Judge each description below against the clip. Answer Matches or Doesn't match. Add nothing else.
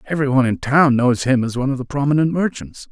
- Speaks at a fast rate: Matches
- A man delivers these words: Matches